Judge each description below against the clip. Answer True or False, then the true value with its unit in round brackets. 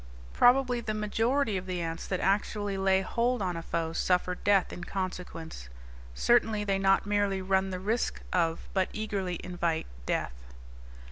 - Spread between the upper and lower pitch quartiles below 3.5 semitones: True (2.8 semitones)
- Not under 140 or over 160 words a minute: True (155 wpm)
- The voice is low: False (195 Hz)